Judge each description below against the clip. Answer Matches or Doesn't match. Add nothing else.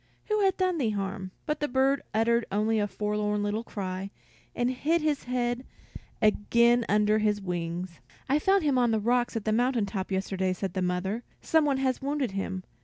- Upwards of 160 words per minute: Matches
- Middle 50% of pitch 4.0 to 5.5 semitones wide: Matches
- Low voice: Doesn't match